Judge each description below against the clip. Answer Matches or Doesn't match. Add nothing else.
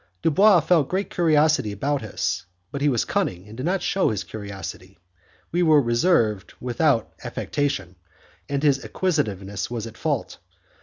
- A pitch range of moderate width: Doesn't match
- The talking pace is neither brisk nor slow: Matches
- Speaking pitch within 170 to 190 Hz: Doesn't match